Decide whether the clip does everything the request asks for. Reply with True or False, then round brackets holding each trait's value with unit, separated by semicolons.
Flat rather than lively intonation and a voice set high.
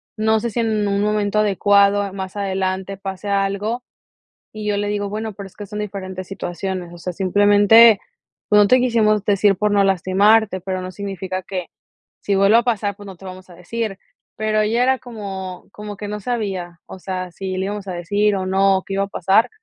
True (1.8 semitones; 200 Hz)